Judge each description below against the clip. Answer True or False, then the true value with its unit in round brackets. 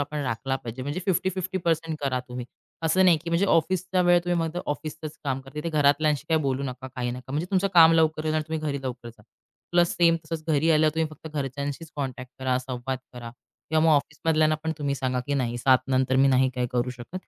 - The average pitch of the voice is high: False (145 Hz)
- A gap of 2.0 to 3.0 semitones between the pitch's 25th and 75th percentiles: False (3.8 semitones)